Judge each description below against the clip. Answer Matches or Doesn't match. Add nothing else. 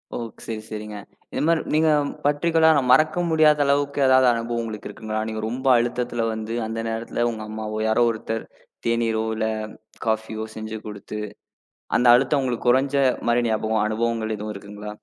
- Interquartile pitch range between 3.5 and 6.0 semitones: Doesn't match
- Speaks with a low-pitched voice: Matches